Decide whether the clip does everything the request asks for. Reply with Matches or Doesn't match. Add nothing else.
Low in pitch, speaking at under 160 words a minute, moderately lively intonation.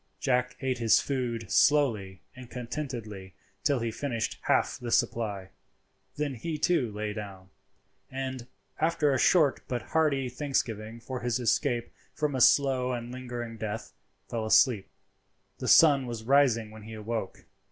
Matches